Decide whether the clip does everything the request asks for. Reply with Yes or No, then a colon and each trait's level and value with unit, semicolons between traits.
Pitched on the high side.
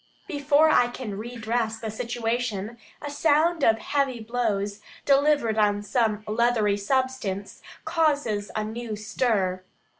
Yes: high, 230 Hz